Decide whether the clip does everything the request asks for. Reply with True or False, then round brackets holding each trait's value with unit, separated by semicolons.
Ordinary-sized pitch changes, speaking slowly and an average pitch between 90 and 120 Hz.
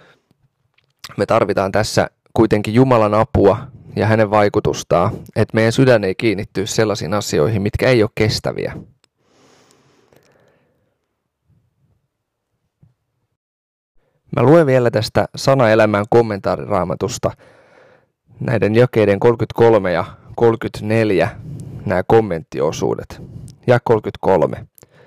True (3.2 semitones; 85 wpm; 115 Hz)